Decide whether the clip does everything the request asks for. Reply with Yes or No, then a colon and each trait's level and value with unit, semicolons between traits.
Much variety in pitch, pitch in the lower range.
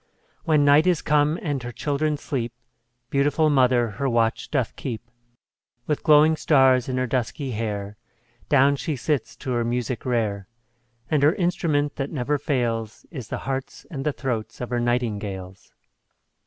No: average, 3.8 semitones; low, 130 Hz